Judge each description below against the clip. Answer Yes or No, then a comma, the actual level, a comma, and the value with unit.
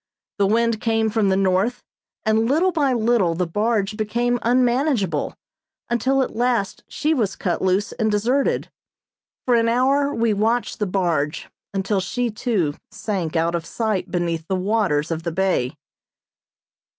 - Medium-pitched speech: No, high, 215 Hz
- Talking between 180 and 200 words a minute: No, average, 150 wpm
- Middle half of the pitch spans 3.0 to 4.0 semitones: No, average, 4.5 semitones